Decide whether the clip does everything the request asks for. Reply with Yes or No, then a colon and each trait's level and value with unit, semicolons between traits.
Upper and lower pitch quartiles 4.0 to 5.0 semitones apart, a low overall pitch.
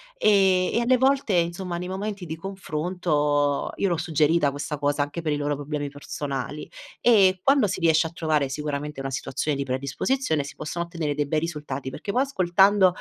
No: average, 4.5 semitones; medium, 160 Hz